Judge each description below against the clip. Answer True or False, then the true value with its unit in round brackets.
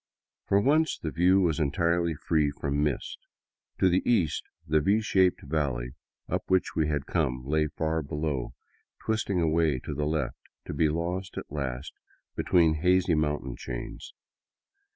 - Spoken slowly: False (160 wpm)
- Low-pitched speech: True (80 Hz)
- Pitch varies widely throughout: False (3.5 semitones)